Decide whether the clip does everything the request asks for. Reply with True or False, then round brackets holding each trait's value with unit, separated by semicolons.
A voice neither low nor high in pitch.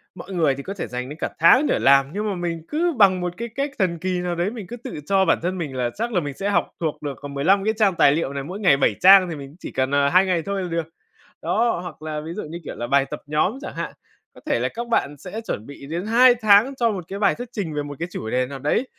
True (175 Hz)